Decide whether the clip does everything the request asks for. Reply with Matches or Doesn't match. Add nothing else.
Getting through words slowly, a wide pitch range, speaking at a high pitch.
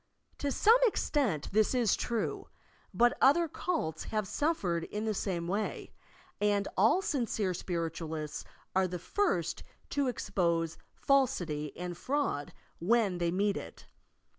Matches